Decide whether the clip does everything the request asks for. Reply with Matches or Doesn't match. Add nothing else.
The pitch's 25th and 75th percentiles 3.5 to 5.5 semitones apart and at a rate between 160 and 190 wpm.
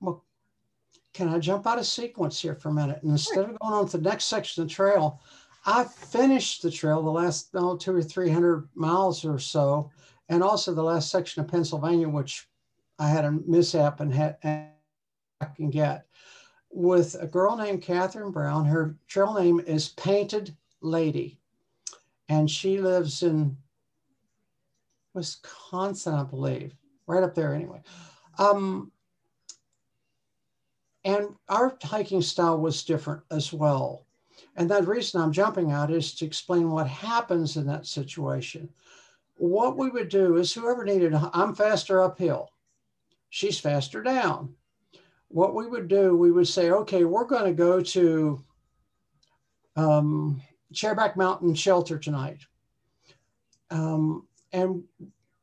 Doesn't match